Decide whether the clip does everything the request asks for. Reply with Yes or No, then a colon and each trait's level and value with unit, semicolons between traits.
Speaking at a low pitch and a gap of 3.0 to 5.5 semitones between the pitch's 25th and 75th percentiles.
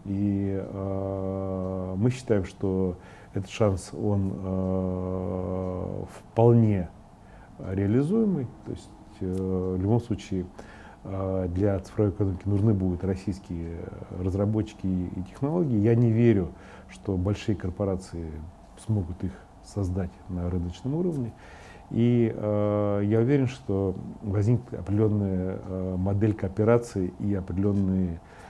No: very low, 95 Hz; narrow, 2.4 semitones